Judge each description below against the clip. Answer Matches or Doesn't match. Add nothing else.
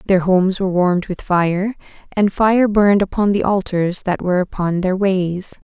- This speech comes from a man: Doesn't match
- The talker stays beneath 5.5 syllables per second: Matches